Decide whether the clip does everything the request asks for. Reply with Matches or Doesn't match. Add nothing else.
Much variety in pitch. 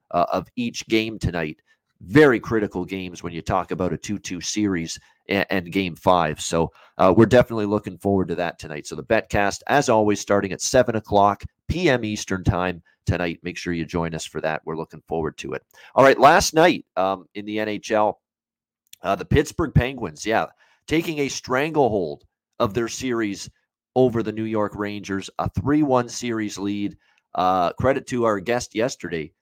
Doesn't match